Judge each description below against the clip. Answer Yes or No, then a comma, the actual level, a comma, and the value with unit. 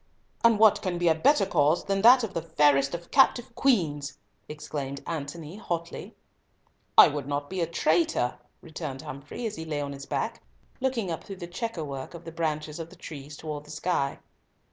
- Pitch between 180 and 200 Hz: No, medium, 160 Hz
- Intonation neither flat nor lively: Yes, average, 4.3 semitones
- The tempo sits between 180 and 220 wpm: Yes, average, 190 wpm